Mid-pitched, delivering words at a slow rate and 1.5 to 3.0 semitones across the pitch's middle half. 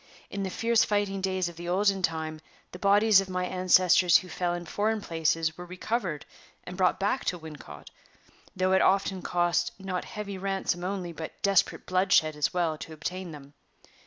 No: medium, 180 Hz; average, 180 wpm; narrow, 2.5 semitones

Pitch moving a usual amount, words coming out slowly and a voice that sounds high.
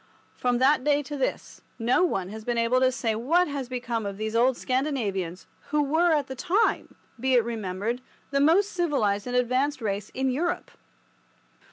No: average, 4.3 semitones; average, 180 wpm; very high, 255 Hz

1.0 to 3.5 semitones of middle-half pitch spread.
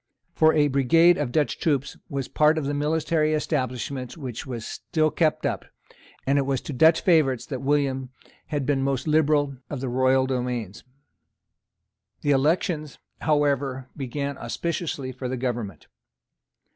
Yes: average, 2.9 semitones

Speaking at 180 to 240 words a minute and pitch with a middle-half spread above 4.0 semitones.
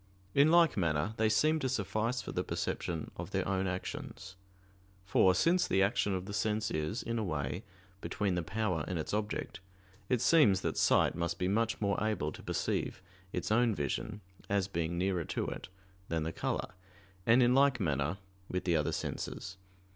Yes: average, 185 wpm; average, 4.6 semitones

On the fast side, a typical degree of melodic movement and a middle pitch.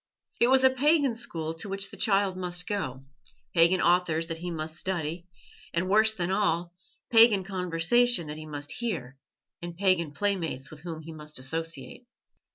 No: average, 165 wpm; average, 3.9 semitones; medium, 175 Hz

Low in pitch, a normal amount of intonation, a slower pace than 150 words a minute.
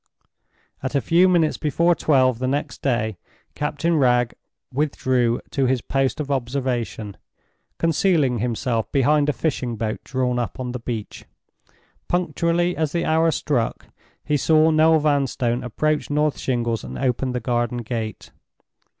Yes: low, 130 Hz; average, 4.0 semitones; average, 140 wpm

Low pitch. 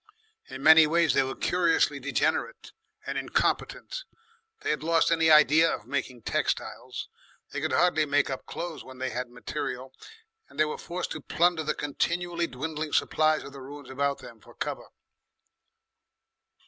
No: medium, 155 Hz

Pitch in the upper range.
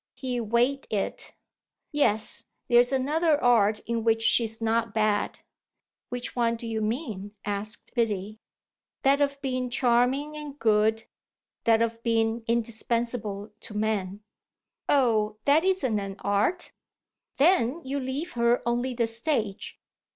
Yes: high, 235 Hz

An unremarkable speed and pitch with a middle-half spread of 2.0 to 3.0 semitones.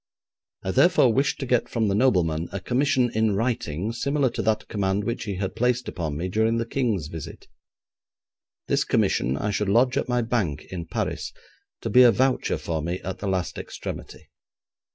No: average, 185 wpm; average, 5.1 semitones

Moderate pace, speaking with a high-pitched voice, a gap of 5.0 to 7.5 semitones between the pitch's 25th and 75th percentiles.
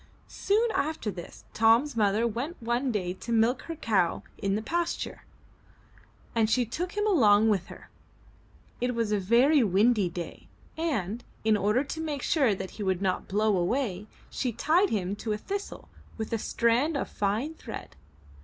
Yes: average, 170 wpm; high, 230 Hz; wide, 5.5 semitones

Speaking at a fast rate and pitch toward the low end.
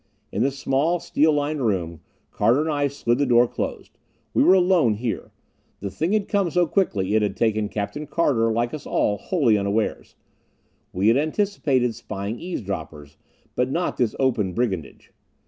No: average, 165 wpm; low, 125 Hz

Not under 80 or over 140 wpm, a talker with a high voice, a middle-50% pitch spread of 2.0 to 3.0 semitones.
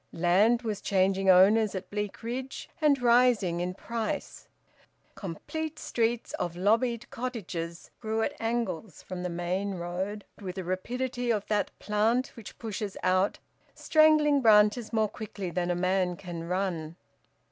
No: slow, 135 wpm; high, 205 Hz; average, 4.3 semitones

